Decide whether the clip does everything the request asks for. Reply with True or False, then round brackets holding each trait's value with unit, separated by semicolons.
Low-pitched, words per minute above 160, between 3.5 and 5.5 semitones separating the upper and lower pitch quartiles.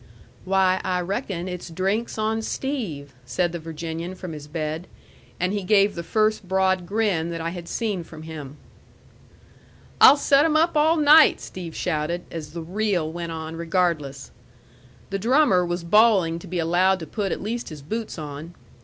False (180 Hz; 170 wpm; 4.3 semitones)